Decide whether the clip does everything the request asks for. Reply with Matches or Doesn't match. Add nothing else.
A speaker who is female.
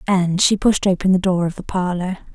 Matches